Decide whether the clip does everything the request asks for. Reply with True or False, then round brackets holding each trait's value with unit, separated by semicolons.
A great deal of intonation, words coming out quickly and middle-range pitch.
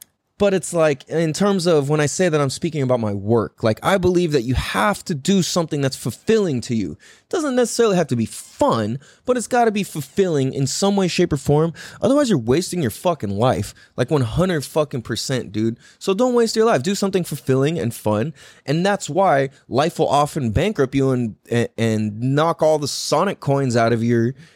True (6.6 semitones; 210 wpm; 150 Hz)